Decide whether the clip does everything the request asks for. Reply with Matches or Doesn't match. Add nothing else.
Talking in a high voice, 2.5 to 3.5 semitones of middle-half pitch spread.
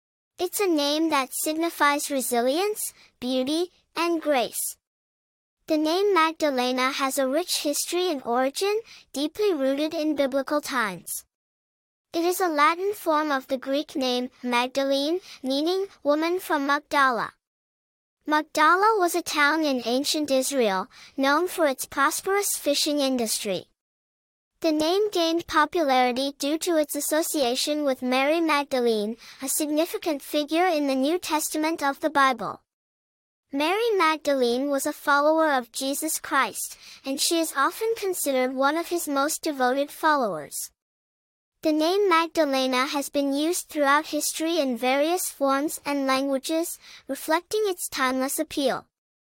Matches